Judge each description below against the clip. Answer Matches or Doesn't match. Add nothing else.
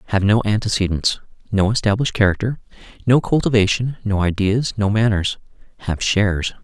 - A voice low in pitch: Matches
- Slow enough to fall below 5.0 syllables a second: Doesn't match